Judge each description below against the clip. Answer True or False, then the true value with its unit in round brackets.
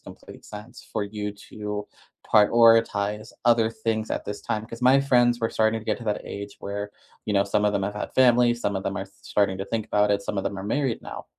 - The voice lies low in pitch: True (105 Hz)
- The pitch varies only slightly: True (2.1 semitones)